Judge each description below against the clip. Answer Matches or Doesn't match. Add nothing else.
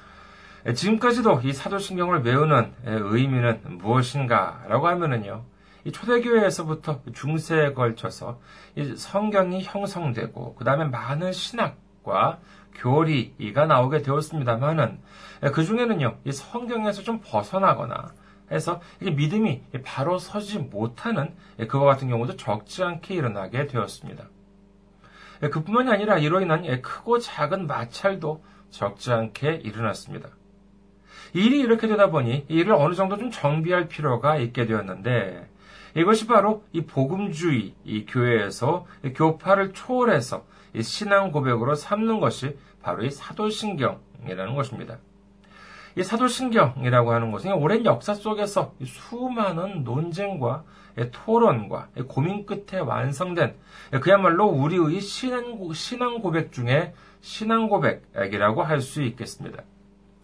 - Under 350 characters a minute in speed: Matches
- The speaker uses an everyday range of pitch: Doesn't match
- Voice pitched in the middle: Matches